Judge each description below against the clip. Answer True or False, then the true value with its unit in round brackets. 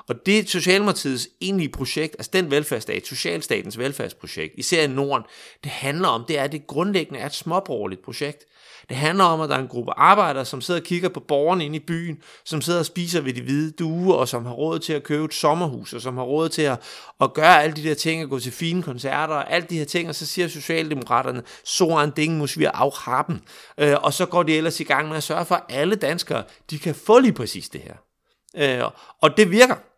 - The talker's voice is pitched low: False (155 Hz)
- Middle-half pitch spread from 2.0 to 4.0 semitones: True (3.3 semitones)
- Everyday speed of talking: False (230 wpm)